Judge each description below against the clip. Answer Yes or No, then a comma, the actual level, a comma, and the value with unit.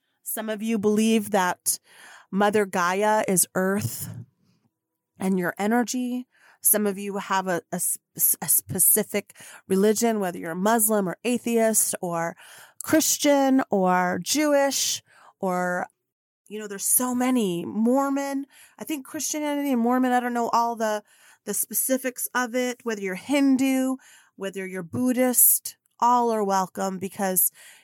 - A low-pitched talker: No, high, 215 Hz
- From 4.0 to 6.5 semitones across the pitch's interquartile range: Yes, average, 4.8 semitones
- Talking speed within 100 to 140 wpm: Yes, slow, 135 wpm